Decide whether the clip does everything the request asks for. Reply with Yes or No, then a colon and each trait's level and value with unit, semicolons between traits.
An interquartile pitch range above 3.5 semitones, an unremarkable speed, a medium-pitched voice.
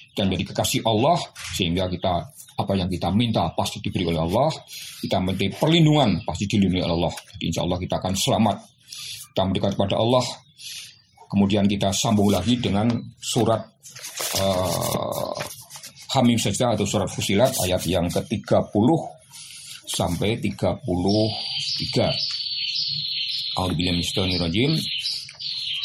No: average, 5.2 semitones; average, 115 wpm; low, 105 Hz